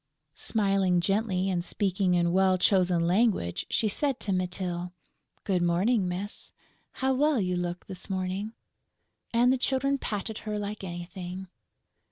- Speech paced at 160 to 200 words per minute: No, average, 140 wpm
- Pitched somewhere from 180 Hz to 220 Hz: Yes, high, 190 Hz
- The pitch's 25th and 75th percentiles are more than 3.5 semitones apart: No, average, 3.2 semitones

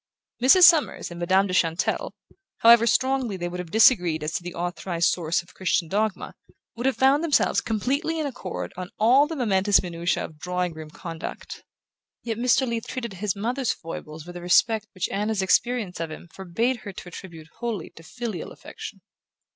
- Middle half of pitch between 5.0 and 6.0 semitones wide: Yes, wide, 5.6 semitones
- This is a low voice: No, high, 195 Hz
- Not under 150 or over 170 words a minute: No, average, 180 wpm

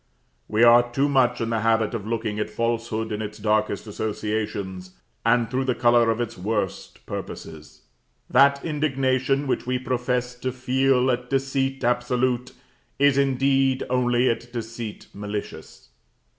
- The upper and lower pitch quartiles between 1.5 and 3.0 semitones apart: Yes, average, 2.7 semitones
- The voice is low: Yes, low, 120 Hz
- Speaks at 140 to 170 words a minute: Yes, average, 145 wpm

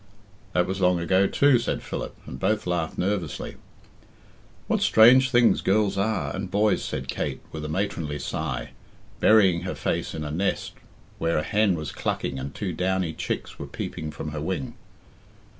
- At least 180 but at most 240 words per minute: No, average, 170 wpm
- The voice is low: Yes, very low, 90 Hz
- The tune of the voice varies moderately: Yes, average, 4.8 semitones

